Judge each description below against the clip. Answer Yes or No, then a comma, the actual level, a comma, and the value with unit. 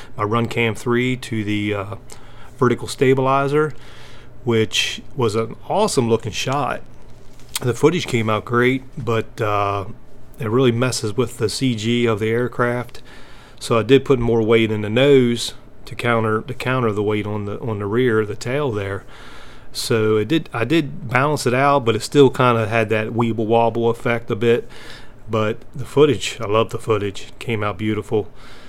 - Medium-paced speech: Yes, average, 175 wpm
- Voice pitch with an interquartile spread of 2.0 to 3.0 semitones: Yes, narrow, 2.6 semitones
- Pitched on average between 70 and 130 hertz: Yes, low, 115 Hz